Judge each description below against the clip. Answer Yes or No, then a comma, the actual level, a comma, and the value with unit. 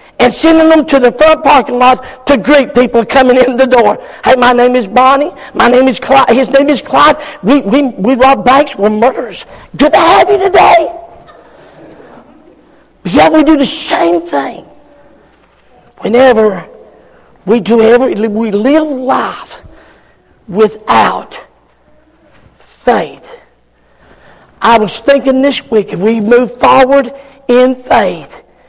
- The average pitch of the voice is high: Yes, very high, 255 Hz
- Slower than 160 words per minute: Yes, average, 140 wpm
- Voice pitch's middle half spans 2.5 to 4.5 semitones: Yes, average, 3.0 semitones